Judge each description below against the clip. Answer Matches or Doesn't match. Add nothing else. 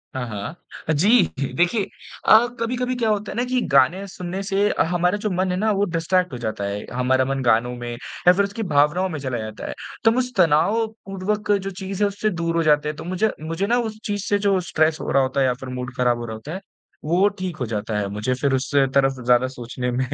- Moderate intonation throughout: Doesn't match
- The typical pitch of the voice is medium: Matches